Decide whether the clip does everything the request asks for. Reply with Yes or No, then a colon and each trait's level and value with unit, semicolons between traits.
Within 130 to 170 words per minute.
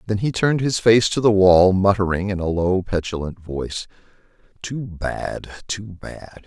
Yes: average, 160 wpm